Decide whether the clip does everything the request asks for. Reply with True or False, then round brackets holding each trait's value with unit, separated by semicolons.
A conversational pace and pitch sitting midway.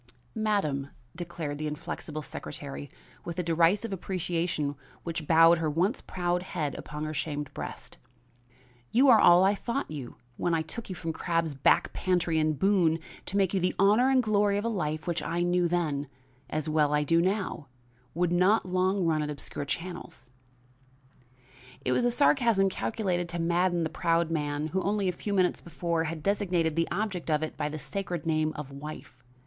True (185 wpm; 170 Hz)